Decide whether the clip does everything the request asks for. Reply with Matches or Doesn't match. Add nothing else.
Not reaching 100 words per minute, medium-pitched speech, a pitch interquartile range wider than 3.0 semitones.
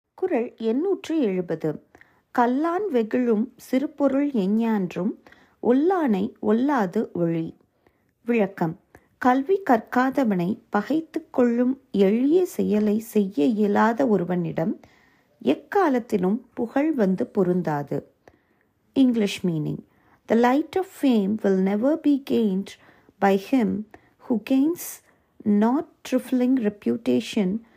Doesn't match